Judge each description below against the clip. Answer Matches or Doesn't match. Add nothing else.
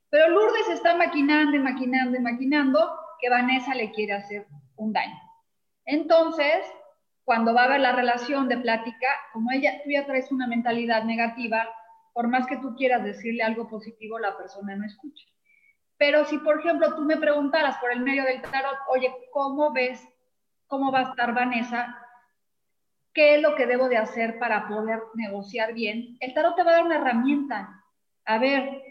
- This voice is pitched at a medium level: Doesn't match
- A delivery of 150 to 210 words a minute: Matches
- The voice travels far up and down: Doesn't match